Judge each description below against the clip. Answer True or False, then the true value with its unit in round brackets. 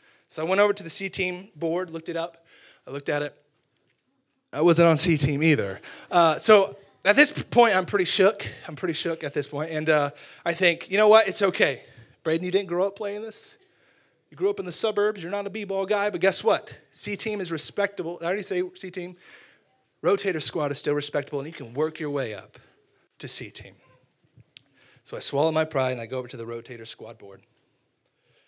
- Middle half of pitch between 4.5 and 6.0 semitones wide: True (5.1 semitones)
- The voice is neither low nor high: True (170 Hz)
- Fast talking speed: True (220 wpm)